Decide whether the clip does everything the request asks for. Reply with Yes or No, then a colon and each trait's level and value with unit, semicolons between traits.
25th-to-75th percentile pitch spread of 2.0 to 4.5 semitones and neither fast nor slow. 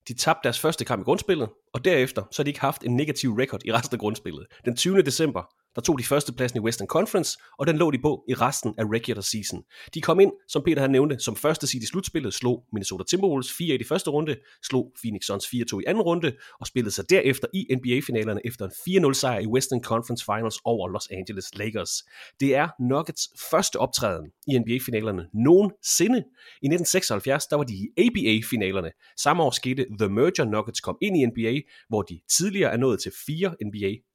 No: average, 5.0 semitones; average, 210 wpm